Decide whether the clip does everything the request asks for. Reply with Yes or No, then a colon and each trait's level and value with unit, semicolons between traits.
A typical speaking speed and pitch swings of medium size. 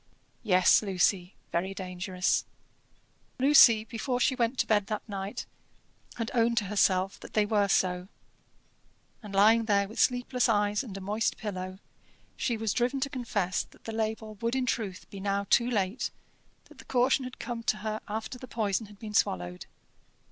Yes: average, 170 wpm; average, 3.3 semitones